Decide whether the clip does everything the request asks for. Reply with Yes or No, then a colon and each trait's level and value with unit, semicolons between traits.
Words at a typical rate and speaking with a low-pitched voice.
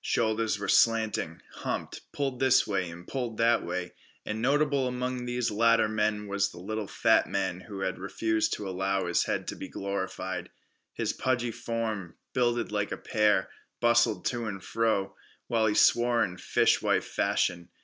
Yes: average, 165 wpm; low, 110 Hz